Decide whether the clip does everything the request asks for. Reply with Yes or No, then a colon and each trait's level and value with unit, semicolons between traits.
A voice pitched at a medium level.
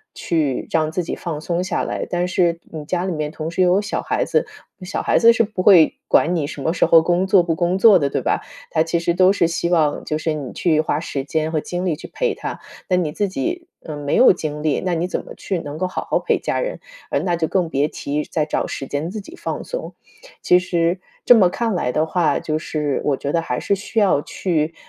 Yes: medium, 170 Hz